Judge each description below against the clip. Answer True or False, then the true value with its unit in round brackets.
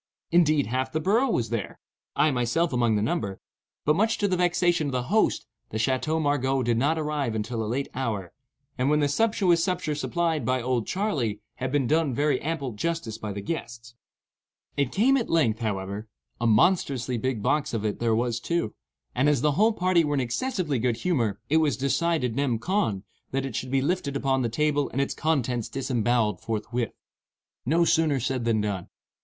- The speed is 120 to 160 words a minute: False (185 wpm)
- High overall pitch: False (135 Hz)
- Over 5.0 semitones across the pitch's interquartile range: True (5.5 semitones)